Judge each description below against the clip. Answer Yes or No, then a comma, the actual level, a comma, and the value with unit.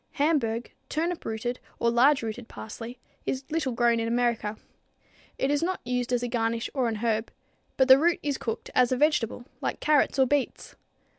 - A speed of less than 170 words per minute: No, average, 180 wpm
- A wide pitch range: No, average, 3.6 semitones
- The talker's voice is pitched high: Yes, high, 245 Hz